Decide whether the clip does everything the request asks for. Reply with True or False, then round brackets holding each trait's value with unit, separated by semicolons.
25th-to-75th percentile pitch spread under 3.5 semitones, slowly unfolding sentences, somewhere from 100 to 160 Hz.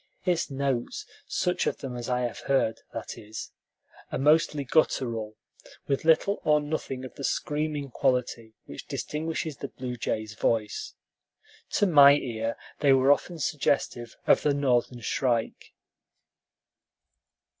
False (3.8 semitones; 130 wpm; 135 Hz)